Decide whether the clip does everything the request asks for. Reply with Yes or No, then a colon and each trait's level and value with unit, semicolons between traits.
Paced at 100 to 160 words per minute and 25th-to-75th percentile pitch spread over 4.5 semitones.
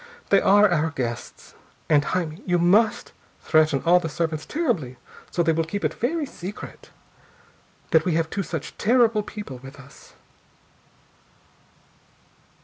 Yes: average, 140 wpm; average, 4.9 semitones